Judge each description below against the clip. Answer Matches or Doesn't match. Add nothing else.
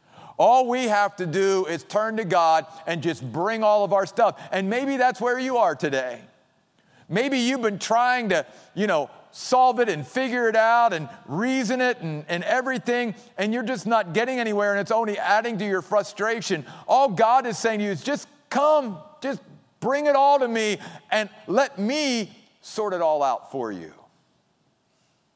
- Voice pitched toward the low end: Doesn't match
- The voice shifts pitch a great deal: Doesn't match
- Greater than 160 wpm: Matches